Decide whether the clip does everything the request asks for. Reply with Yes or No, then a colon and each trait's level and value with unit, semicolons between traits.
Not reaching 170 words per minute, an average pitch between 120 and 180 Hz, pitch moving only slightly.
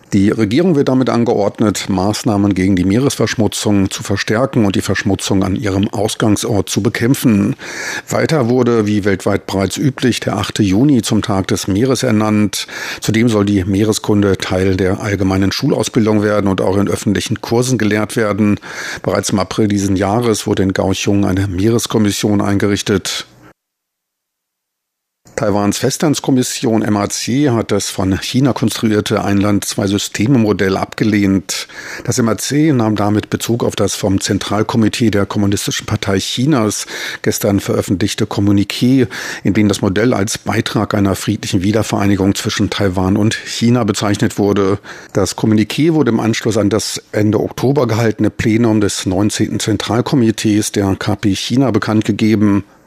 No: average, 135 wpm; low, 105 Hz; narrow, 2.0 semitones